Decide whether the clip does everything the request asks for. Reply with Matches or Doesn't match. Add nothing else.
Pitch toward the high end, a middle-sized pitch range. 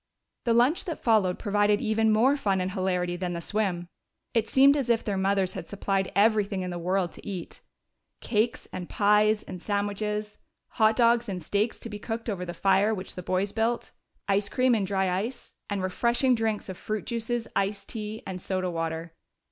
Matches